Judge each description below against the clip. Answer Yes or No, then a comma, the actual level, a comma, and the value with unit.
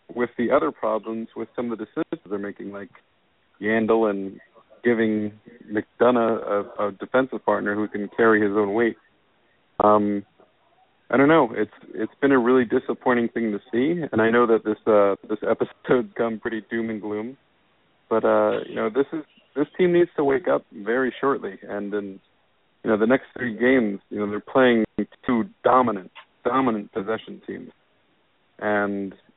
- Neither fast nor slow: Yes, average, 175 wpm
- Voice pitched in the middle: No, low, 110 Hz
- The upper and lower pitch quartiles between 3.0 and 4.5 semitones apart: No, narrow, 2.6 semitones